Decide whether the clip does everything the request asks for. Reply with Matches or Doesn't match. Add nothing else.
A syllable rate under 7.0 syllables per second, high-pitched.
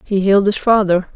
Matches